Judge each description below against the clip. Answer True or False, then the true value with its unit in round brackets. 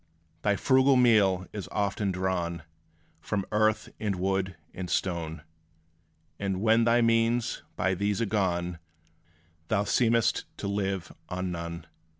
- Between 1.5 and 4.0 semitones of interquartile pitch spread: True (3.1 semitones)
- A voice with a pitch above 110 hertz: False (100 Hz)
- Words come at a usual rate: False (130 wpm)